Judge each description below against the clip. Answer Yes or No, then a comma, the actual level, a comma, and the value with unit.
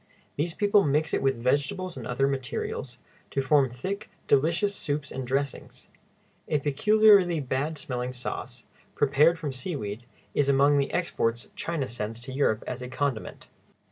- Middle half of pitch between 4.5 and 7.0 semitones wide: No, average, 4.0 semitones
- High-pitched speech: No, medium, 140 Hz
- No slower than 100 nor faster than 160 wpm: Yes, average, 150 wpm